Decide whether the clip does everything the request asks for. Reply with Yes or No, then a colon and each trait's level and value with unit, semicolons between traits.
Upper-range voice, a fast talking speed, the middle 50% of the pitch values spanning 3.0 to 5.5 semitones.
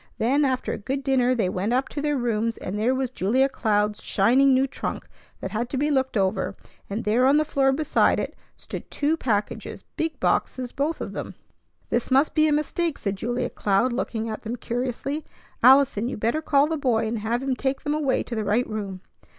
Yes: very high, 250 Hz; fast, 210 wpm; average, 3.9 semitones